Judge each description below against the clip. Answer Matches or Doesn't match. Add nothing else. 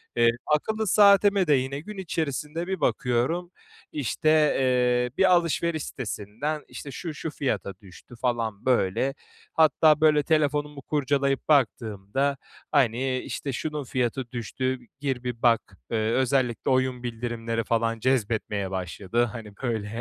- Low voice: Matches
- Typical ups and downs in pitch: Matches